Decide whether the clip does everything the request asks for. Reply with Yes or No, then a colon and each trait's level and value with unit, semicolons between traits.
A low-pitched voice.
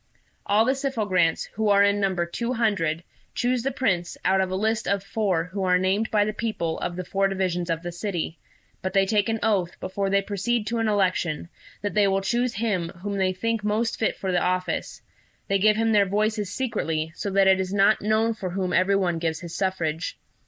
No: high, 195 Hz